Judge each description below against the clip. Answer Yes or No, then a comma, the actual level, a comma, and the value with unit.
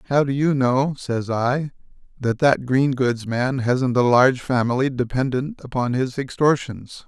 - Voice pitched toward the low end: Yes, low, 130 Hz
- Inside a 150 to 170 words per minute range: Yes, average, 160 wpm